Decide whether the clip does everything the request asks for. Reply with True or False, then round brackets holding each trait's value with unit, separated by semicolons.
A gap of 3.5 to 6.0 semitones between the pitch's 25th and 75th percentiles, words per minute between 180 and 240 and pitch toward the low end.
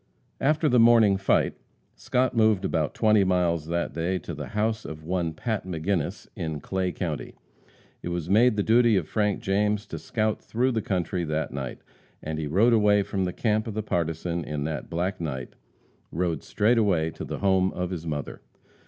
True (4.7 semitones; 185 wpm; 95 Hz)